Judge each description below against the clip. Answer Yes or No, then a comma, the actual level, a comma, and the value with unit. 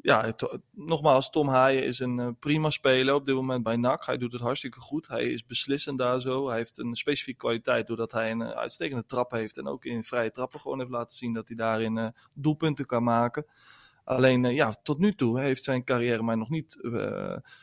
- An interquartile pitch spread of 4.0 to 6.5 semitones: No, average, 2.9 semitones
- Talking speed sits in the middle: No, fast, 225 wpm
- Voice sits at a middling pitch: No, low, 125 Hz